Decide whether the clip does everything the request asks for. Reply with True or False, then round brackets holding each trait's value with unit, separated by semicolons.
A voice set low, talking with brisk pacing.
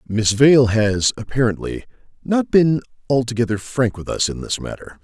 False (120 Hz; 155 wpm)